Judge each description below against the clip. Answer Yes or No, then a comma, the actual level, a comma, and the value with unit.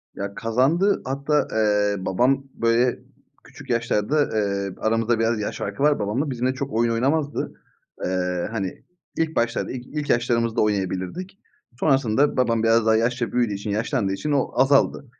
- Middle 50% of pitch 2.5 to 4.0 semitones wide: No, average, 4.4 semitones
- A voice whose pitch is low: Yes, low, 115 Hz